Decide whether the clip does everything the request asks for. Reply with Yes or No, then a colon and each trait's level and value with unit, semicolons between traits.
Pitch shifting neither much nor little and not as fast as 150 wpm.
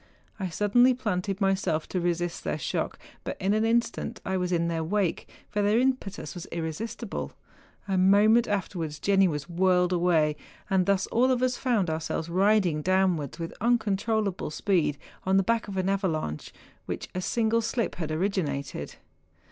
No: average, 3.9 semitones; average, 165 wpm